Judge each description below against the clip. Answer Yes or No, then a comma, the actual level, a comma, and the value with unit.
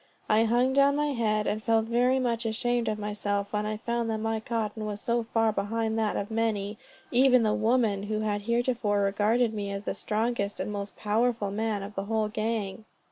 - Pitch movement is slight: Yes, narrow, 2.1 semitones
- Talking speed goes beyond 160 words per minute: Yes, fast, 205 wpm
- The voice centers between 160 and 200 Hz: No, high, 220 Hz